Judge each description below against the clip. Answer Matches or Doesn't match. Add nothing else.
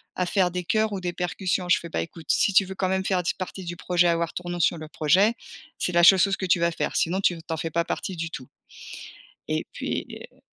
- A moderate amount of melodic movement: Doesn't match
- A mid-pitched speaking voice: Matches